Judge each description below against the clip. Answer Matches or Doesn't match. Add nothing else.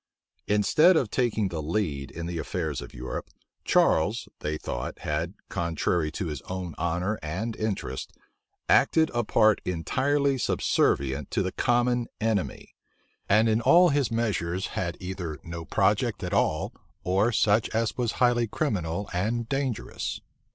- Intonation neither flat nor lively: Doesn't match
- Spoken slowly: Doesn't match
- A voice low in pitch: Matches